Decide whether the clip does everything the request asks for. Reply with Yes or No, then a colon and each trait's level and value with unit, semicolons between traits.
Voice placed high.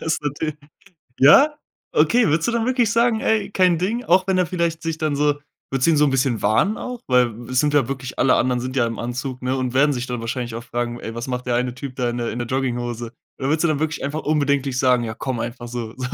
No: low, 135 Hz